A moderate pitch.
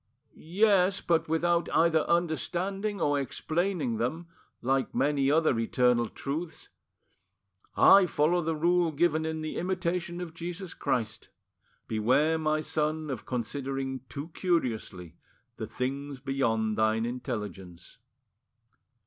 Yes: medium, 155 Hz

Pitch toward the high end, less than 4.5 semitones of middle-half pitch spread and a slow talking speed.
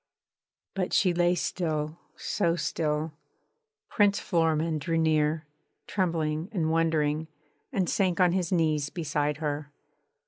No: medium, 160 Hz; narrow, 2.4 semitones; slow, 115 wpm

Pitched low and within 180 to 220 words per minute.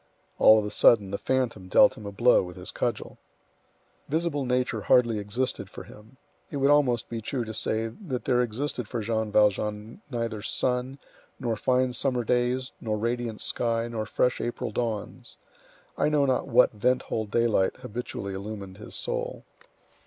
No: low, 115 Hz; average, 165 wpm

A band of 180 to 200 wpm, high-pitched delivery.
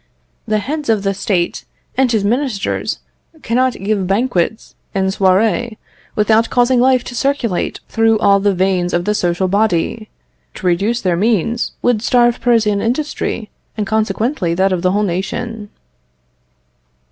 No: average, 145 wpm; high, 215 Hz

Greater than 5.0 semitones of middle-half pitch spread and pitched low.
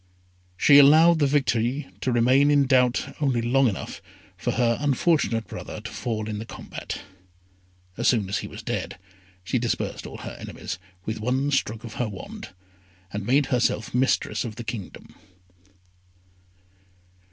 No: average, 3.8 semitones; low, 120 Hz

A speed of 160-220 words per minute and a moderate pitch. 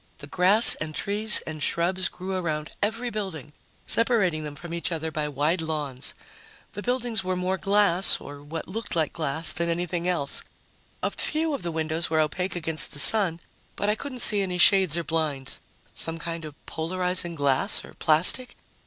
Yes: average, 180 wpm; medium, 170 Hz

